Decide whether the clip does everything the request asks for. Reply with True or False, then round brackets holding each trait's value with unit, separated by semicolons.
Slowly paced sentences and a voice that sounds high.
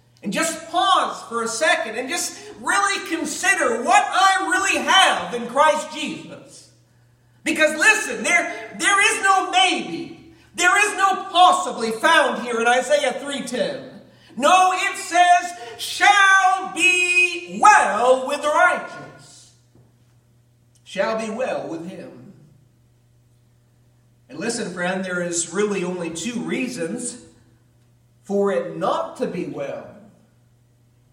True (120 wpm; 260 Hz)